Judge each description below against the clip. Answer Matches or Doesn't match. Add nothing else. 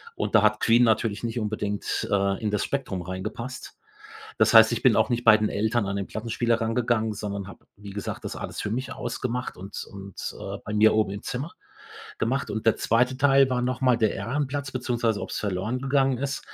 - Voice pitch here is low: Matches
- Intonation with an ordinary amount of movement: Matches